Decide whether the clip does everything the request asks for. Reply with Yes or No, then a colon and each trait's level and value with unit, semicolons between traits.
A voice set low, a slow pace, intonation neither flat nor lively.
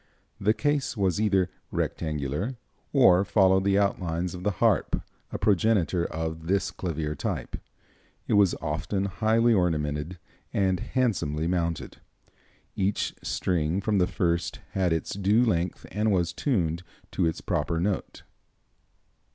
Yes: very low, 95 Hz; slow, 130 wpm; average, 3.6 semitones